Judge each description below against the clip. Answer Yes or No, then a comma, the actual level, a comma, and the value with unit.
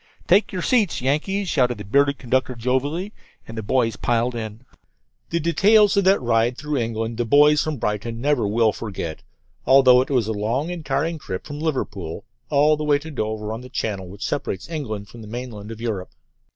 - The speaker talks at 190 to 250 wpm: Yes, average, 195 wpm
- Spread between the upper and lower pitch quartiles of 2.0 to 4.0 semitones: No, average, 5.1 semitones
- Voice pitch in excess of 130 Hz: No, low, 125 Hz